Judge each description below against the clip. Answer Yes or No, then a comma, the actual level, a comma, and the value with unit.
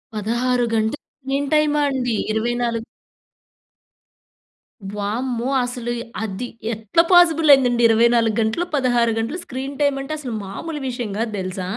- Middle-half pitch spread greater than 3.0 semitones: Yes, average, 3.5 semitones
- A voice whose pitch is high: Yes, high, 240 Hz